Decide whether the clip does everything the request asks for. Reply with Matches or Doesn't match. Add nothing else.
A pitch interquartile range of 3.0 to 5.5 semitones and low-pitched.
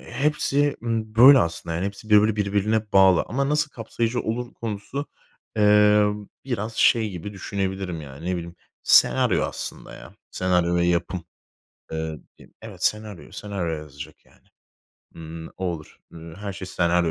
Matches